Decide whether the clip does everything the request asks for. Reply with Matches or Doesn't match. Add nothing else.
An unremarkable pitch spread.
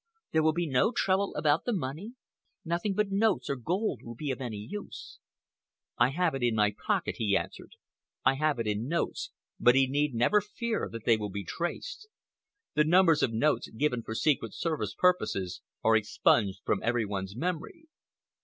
Doesn't match